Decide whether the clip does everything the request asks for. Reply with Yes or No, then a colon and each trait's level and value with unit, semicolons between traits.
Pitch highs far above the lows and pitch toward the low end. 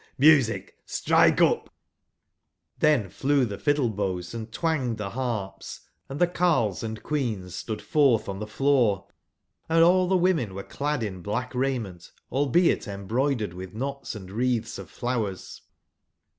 Yes: wide, 5.8 semitones; low, 120 Hz